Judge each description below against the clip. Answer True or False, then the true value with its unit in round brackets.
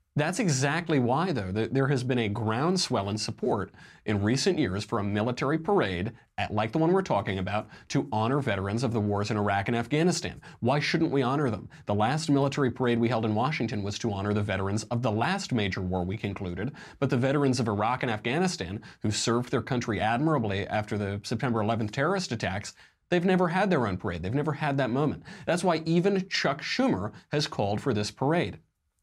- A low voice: True (120 Hz)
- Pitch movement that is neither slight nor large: False (5.9 semitones)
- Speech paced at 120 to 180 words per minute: False (205 wpm)